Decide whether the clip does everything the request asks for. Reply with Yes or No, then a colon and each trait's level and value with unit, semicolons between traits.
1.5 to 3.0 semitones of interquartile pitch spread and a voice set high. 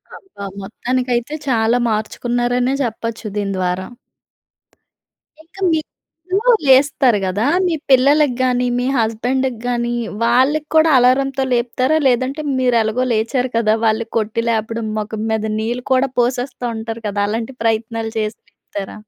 Yes: narrow, 2.6 semitones; high, 240 Hz